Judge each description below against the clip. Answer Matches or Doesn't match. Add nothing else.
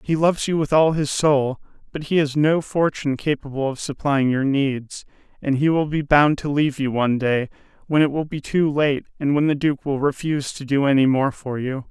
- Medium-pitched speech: Matches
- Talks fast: Matches